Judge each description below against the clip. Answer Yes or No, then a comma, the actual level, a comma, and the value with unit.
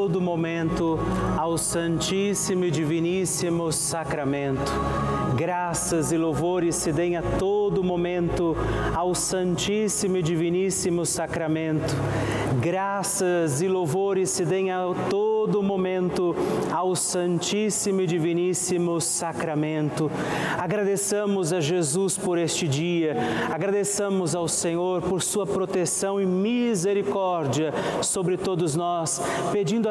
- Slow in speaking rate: Yes, slow, 100 wpm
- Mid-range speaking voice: Yes, medium, 175 Hz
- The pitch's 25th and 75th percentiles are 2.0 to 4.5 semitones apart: Yes, narrow, 2.5 semitones